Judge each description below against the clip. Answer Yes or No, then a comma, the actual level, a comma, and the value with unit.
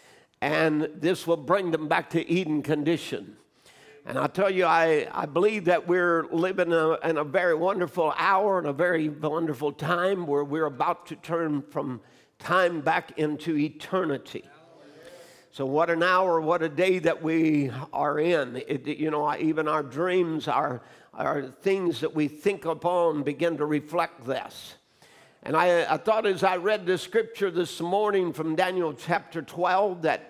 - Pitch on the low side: No, medium, 165 Hz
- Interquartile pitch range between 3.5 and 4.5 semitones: No, average, 2.8 semitones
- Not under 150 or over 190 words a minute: Yes, average, 170 wpm